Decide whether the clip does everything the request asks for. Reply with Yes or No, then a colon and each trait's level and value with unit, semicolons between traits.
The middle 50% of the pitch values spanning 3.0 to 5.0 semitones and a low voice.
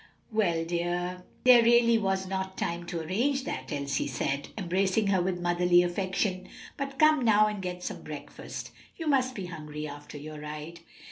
No: average, 4.3 semitones; medium, 185 Hz